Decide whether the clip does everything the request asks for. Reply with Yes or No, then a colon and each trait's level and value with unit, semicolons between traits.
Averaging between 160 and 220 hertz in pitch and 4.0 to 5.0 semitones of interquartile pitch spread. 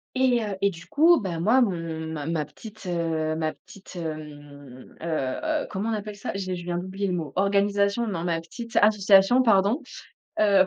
Yes: high, 190 Hz; average, 4.4 semitones